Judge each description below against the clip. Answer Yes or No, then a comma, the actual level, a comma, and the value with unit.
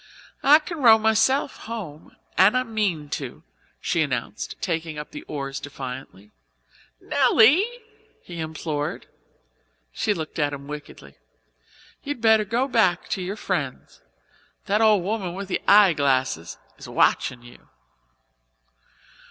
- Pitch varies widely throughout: Yes, wide, 7.2 semitones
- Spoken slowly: Yes, slow, 125 wpm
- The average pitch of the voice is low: No, medium, 180 Hz